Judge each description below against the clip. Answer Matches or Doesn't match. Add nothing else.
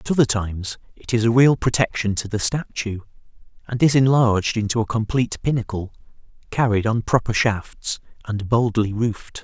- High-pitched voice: Doesn't match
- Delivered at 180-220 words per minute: Doesn't match